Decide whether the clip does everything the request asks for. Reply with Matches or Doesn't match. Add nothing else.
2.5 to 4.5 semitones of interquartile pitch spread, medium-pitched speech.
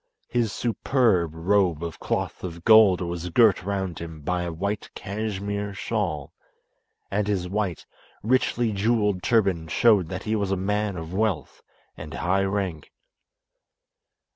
Doesn't match